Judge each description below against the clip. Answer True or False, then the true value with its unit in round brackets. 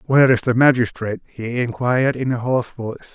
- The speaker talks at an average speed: True (190 wpm)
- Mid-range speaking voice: False (120 Hz)